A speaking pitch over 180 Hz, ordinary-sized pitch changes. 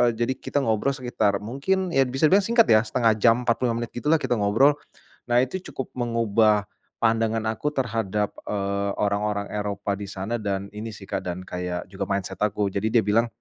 No: low, 110 Hz; average, 3.3 semitones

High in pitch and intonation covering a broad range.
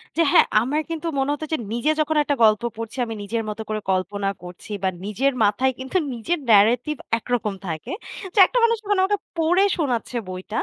Yes: high, 245 Hz; wide, 6.7 semitones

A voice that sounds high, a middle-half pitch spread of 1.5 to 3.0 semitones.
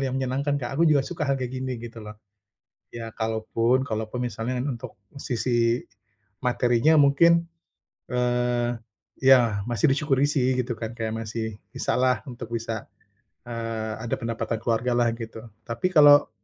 No: low, 120 Hz; narrow, 2.6 semitones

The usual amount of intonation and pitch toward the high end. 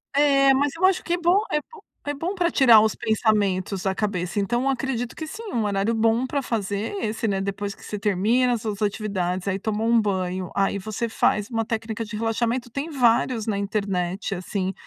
Yes: average, 4.2 semitones; high, 220 Hz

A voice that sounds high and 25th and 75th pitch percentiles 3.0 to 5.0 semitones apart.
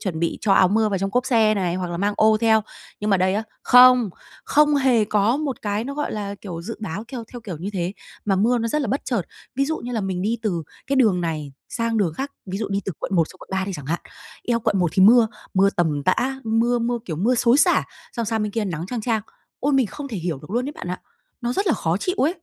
Yes: high, 215 Hz; average, 4.5 semitones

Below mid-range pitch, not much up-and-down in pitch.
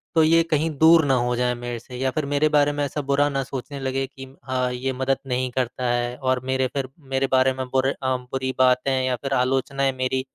Yes: low, 130 Hz; narrow, 1.4 semitones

